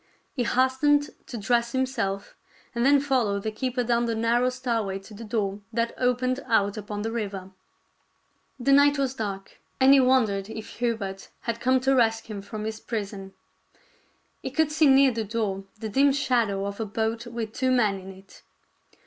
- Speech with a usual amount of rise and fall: Yes, average, 3.9 semitones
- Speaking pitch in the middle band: No, high, 230 Hz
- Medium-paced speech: Yes, average, 185 wpm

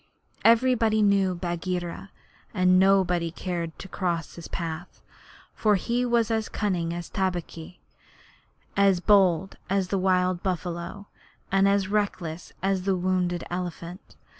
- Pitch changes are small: Yes, narrow, 2.3 semitones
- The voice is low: No, medium, 185 Hz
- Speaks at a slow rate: Yes, slow, 125 wpm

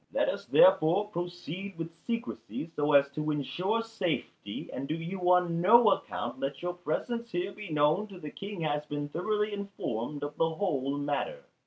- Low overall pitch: No, medium, 170 Hz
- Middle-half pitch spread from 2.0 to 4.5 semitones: No, wide, 5.4 semitones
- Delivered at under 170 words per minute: No, average, 175 wpm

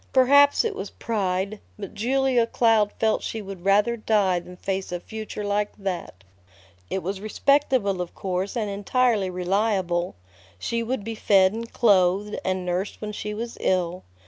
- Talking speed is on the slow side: No, average, 160 wpm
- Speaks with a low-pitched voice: No, high, 205 Hz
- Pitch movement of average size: Yes, average, 3.3 semitones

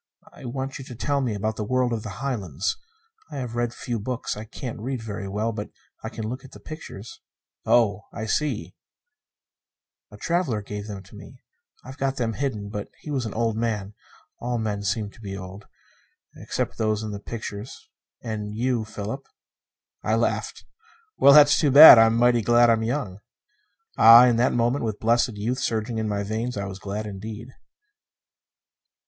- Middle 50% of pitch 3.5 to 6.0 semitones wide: No, average, 3.1 semitones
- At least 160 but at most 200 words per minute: Yes, average, 185 wpm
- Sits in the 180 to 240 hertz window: No, low, 115 Hz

